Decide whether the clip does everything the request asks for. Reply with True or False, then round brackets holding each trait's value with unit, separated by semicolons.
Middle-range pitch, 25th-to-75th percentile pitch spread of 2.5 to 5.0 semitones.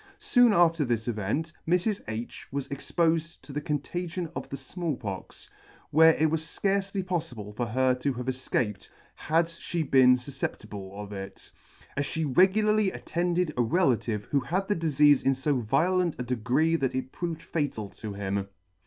False (145 Hz; 5.6 semitones)